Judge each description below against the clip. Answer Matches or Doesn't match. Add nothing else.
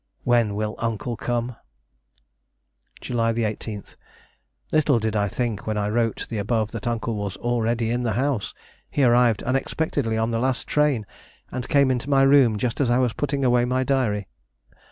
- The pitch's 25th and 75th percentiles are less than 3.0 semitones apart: Matches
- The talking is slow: Doesn't match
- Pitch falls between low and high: Doesn't match